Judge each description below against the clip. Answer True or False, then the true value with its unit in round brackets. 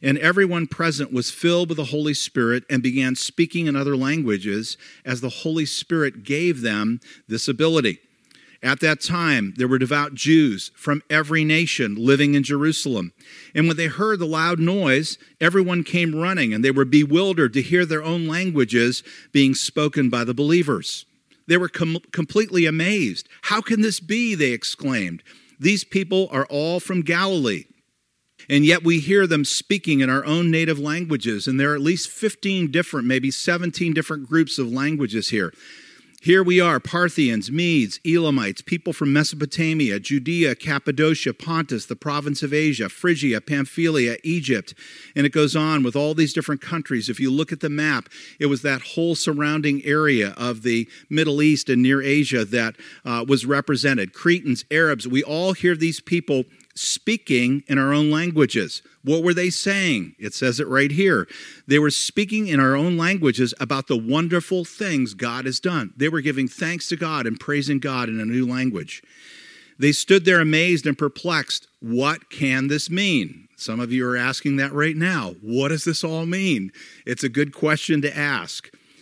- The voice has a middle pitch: True (150 Hz)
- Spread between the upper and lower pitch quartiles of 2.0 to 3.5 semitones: False (3.9 semitones)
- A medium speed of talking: True (175 wpm)